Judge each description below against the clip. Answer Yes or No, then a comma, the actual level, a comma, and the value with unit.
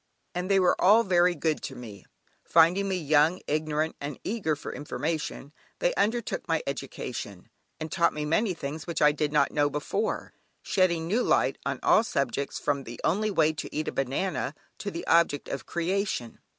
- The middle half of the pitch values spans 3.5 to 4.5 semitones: Yes, average, 4.2 semitones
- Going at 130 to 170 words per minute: No, average, 180 wpm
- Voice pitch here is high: No, medium, 160 Hz